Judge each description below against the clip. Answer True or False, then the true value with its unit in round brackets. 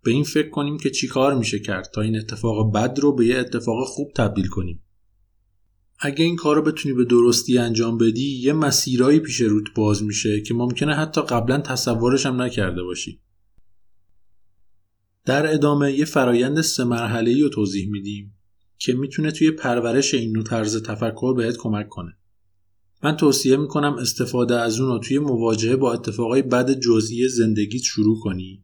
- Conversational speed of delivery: False (165 wpm)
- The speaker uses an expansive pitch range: False (4.6 semitones)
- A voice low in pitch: True (120 Hz)